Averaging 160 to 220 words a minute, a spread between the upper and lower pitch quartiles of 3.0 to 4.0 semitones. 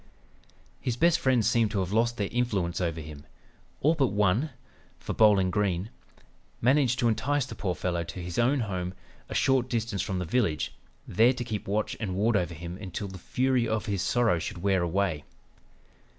No: average, 185 wpm; average, 4.9 semitones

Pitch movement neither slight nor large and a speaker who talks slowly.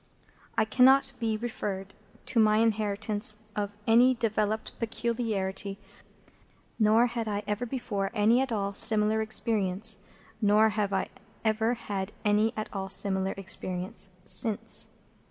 No: narrow, 2.0 semitones; slow, 125 wpm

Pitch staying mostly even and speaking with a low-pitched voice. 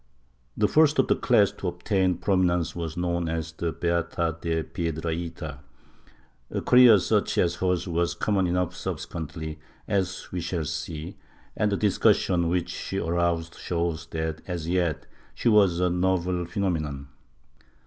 Yes: narrow, 2.1 semitones; very low, 85 Hz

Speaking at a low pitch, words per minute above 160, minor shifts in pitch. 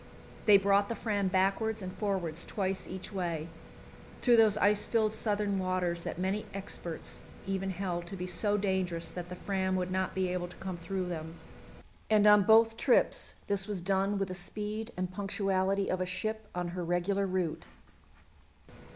No: high, 190 Hz; average, 175 wpm; narrow, 2.1 semitones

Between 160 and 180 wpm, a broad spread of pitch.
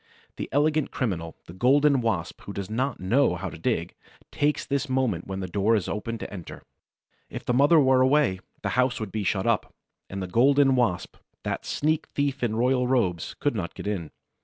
No: average, 200 wpm; wide, 6.0 semitones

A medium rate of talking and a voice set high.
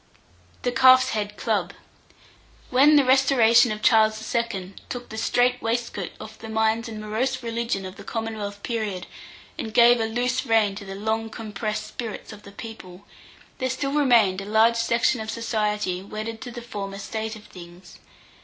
Yes: average, 170 wpm; high, 220 Hz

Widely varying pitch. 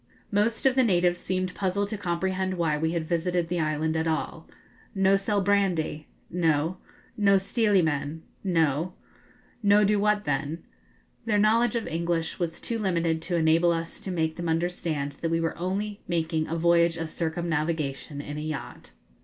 No: average, 3.3 semitones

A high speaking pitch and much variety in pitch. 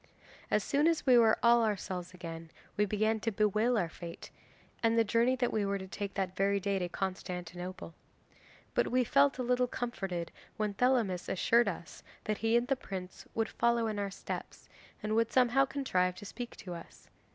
No: high, 210 Hz; average, 4.2 semitones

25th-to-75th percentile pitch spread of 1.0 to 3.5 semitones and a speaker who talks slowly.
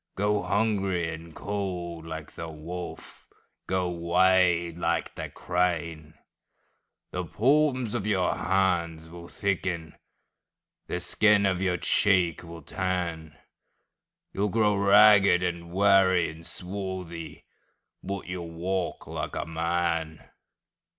Yes: average, 2.7 semitones; slow, 105 wpm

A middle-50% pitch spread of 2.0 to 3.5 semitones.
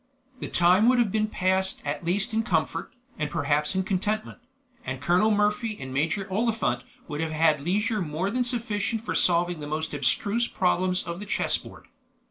No: average, 5.3 semitones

